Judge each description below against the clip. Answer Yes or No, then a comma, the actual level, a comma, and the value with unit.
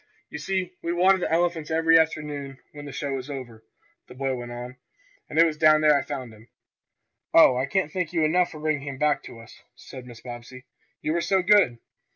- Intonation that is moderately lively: Yes, average, 4.2 semitones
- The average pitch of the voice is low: No, medium, 150 Hz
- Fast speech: Yes, fast, 215 wpm